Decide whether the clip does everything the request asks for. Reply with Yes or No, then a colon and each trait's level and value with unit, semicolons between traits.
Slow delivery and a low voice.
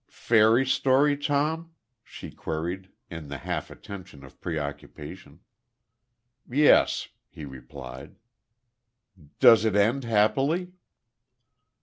Yes: slow, 90 wpm; low, 110 Hz